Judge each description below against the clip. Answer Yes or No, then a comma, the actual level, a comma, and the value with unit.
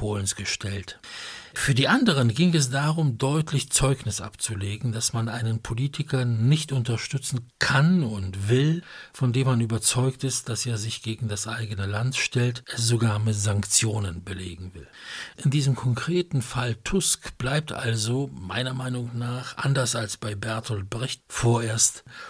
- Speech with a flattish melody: No, average, 3.3 semitones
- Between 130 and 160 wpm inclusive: Yes, average, 145 wpm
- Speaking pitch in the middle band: No, low, 120 Hz